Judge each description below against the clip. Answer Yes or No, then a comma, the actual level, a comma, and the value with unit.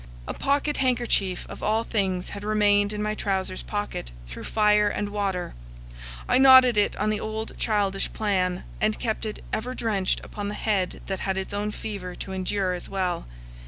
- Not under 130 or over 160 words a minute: No, average, 180 wpm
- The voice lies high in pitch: Yes, high, 205 Hz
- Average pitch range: No, narrow, 2.1 semitones